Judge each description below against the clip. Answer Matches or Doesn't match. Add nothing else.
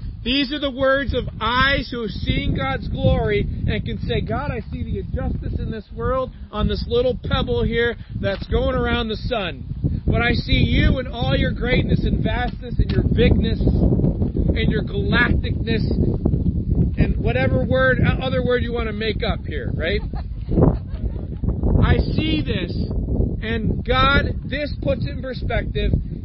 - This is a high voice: Matches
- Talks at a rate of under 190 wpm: Matches